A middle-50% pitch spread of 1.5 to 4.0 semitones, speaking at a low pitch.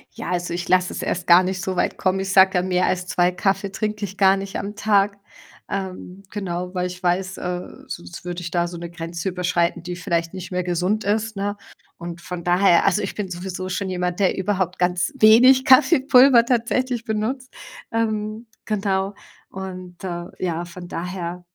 No: narrow, 2.4 semitones; medium, 185 Hz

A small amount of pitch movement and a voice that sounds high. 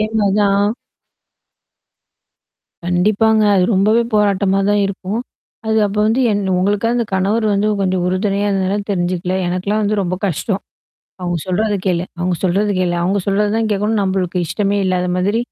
Yes: narrow, 2.3 semitones; high, 200 Hz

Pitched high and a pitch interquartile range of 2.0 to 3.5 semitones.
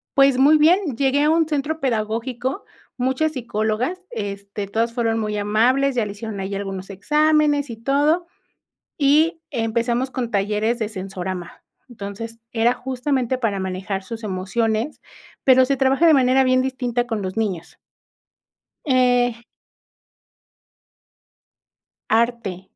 No: high, 235 Hz; average, 4.3 semitones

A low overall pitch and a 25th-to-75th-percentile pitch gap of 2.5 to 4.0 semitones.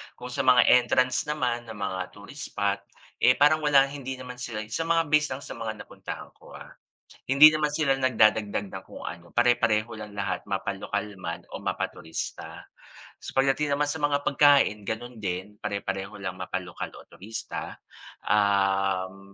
No: low, 115 Hz; wide, 5.6 semitones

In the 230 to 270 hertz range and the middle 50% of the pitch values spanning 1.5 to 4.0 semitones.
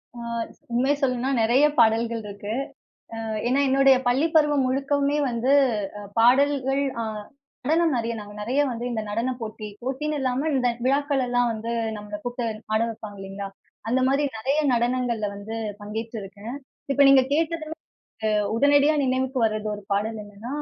Yes: high, 245 Hz; average, 3.7 semitones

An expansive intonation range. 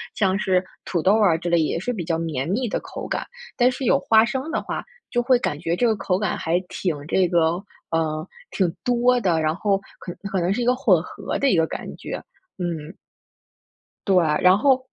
Yes: wide, 6.1 semitones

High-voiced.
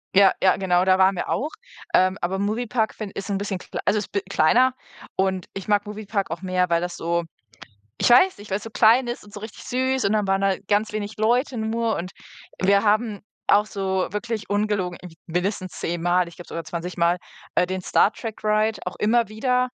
Yes: high, 200 Hz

